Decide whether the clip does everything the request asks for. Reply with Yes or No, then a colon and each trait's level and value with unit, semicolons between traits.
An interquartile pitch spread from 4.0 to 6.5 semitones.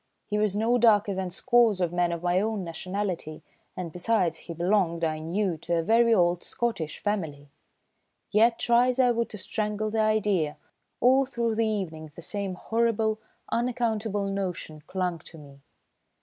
Yes: average, 4.6 semitones